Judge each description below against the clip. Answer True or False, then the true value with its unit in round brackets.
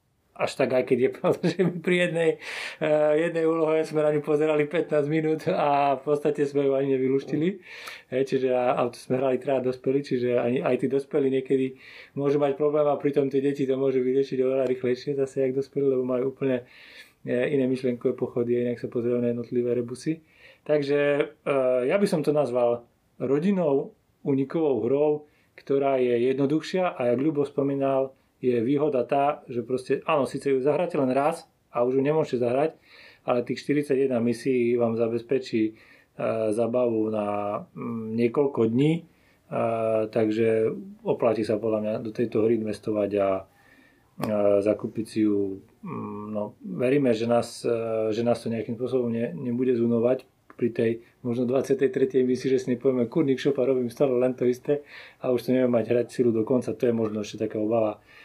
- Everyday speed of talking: False (170 wpm)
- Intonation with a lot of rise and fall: False (3.1 semitones)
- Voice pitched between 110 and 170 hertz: True (130 Hz)